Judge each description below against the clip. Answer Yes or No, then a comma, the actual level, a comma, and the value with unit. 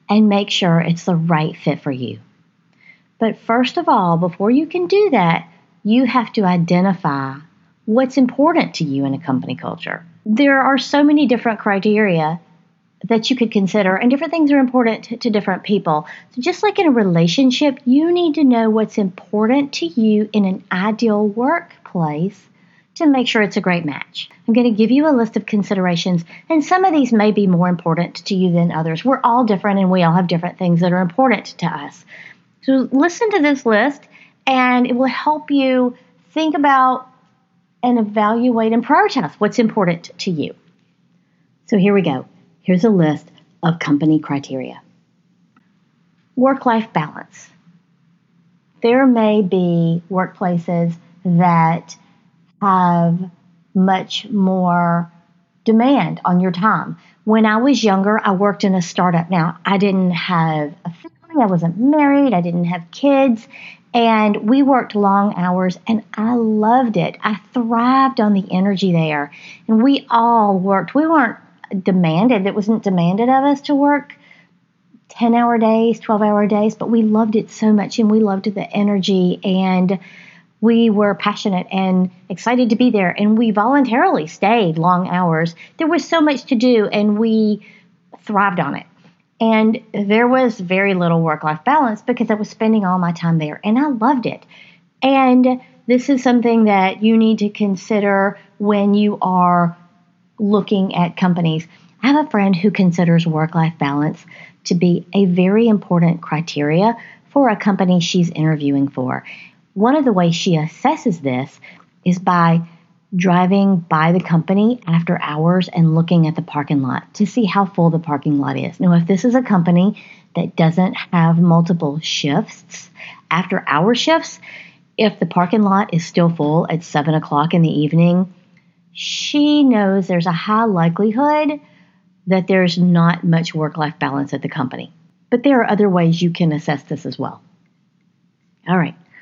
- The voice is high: Yes, high, 195 Hz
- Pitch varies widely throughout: No, average, 4.8 semitones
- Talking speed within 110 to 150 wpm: No, average, 170 wpm